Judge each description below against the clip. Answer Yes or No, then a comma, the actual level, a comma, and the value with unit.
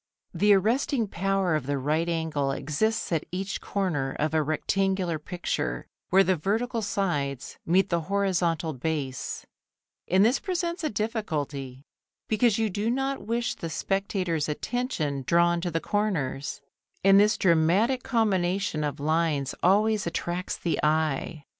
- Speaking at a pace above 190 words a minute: No, average, 140 wpm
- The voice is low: No, medium, 180 Hz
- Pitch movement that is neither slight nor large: Yes, average, 5.0 semitones